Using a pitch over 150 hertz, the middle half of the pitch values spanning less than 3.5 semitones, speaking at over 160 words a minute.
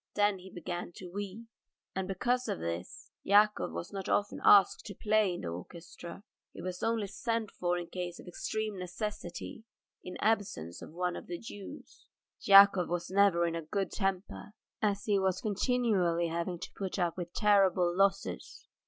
Yes: high, 190 Hz; average, 2.8 semitones; average, 175 wpm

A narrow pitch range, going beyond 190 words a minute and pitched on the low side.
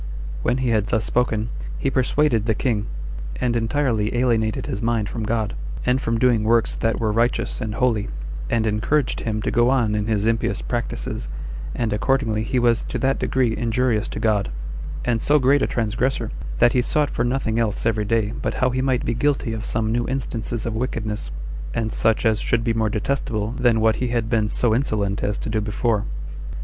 Yes: narrow, 2.3 semitones; average, 200 wpm; low, 115 Hz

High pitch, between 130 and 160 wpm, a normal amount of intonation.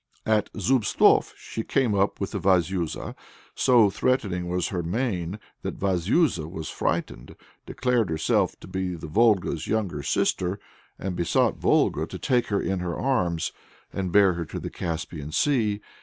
No: very low, 95 Hz; average, 145 wpm; average, 4.2 semitones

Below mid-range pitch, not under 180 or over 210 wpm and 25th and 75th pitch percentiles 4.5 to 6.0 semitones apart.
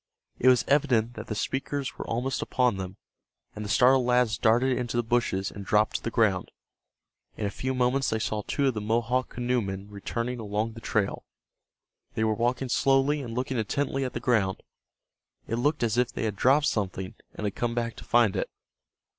No: low, 120 Hz; average, 195 wpm; average, 3.0 semitones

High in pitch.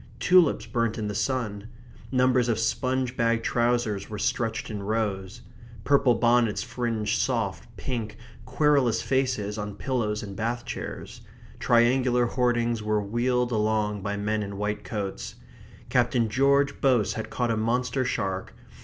No: low, 115 Hz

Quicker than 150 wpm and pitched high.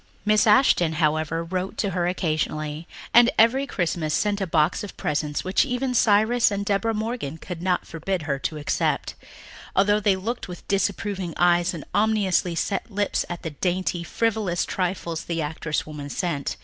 No: average, 165 wpm; medium, 180 Hz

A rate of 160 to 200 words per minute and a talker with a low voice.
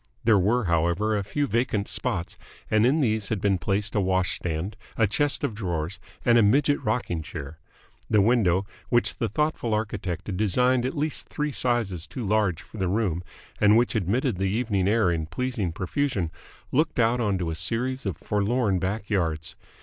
Yes: average, 180 wpm; low, 105 Hz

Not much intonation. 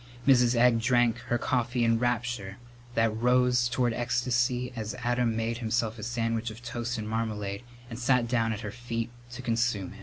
Yes: narrow, 1.4 semitones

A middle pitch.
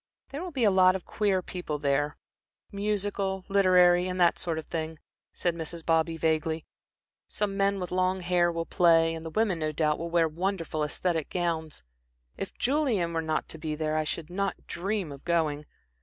Yes: medium, 170 Hz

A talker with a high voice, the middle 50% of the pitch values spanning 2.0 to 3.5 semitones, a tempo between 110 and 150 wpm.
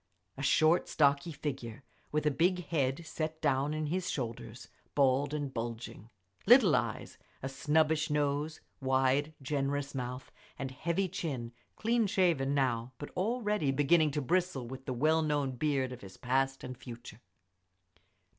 No: medium, 145 Hz; average, 3.2 semitones; average, 145 wpm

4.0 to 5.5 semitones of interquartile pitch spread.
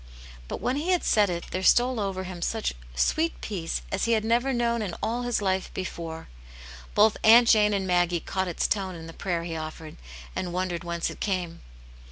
Yes: average, 4.5 semitones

